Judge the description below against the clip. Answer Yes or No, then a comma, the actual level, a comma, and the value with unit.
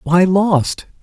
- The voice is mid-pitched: Yes, medium, 180 Hz